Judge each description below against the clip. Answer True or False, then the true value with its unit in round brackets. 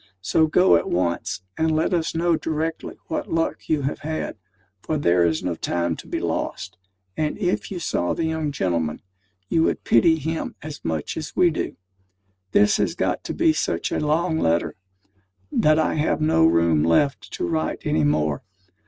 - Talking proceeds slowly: False (180 wpm)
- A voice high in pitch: False (150 Hz)